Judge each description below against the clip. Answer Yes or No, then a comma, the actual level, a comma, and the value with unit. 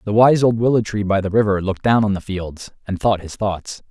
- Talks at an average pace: No, fast, 260 wpm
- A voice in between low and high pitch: No, low, 105 Hz